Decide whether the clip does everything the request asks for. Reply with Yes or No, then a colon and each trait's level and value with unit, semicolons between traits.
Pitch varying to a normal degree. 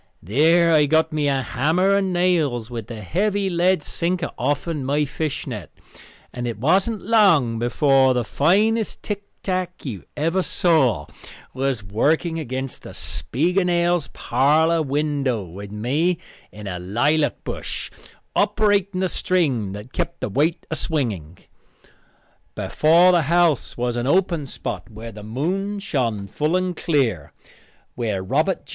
No: wide, 6.5 semitones